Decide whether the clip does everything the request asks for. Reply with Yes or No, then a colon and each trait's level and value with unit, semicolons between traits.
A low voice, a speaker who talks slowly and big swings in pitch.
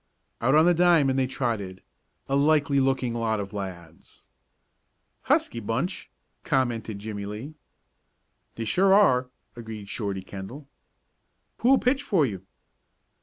Yes: low, 120 Hz; slow, 125 wpm; wide, 6.1 semitones